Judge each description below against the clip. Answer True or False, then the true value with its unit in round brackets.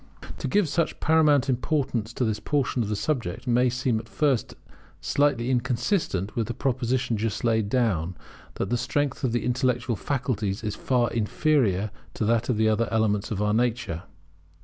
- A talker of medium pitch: False (120 Hz)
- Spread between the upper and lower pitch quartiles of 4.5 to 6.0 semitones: False (3.3 semitones)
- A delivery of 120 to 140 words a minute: False (170 wpm)